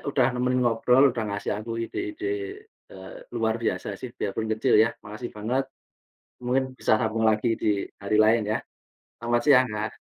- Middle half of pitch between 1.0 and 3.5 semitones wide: Yes, average, 2.7 semitones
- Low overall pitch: Yes, low, 120 Hz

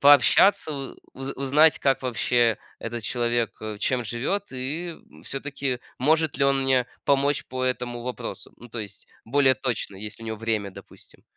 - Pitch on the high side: No, low, 125 Hz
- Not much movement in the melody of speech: No, average, 3.2 semitones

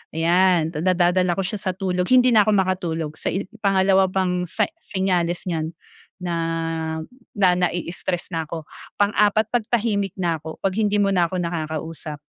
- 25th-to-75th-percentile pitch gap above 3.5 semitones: No, average, 2.7 semitones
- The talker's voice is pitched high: No, medium, 180 Hz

